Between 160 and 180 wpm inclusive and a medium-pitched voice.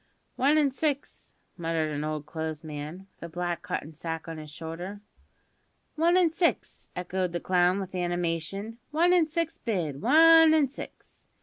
Yes: average, 165 wpm; medium, 180 Hz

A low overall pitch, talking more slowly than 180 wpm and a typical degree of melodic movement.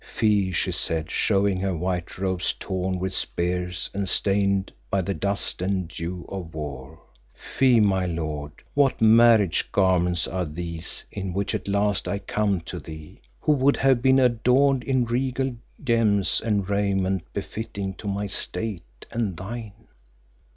Yes: low, 100 Hz; average, 150 wpm; average, 3.7 semitones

